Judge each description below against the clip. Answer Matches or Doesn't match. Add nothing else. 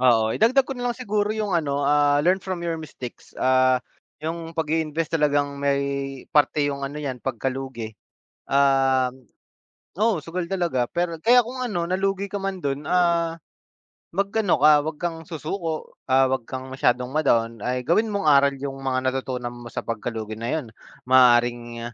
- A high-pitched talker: Doesn't match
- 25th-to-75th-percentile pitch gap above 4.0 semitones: Matches